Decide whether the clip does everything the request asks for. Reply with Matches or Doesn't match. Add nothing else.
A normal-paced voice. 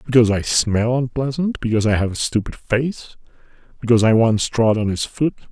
Matches